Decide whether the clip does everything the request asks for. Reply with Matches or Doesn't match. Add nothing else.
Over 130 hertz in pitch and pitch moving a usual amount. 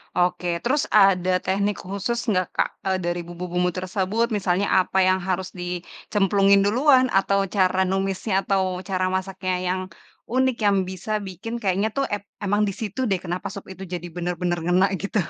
Doesn't match